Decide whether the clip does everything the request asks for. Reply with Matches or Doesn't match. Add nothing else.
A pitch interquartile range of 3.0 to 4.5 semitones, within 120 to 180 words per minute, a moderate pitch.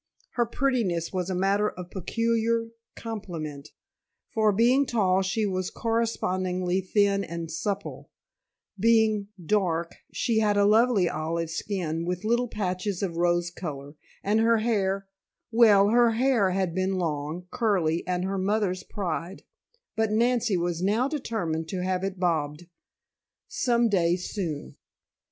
Doesn't match